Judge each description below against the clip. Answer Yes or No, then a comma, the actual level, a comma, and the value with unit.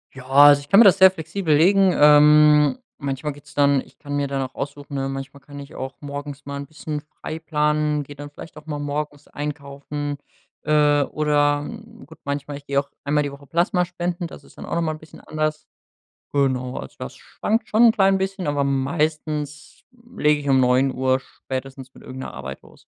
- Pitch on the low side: No, medium, 145 Hz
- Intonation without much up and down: Yes, narrow, 1.7 semitones